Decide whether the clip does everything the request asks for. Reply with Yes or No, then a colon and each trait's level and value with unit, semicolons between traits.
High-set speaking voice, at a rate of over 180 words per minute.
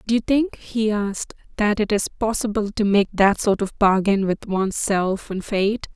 Yes: high, 205 Hz; average, 200 wpm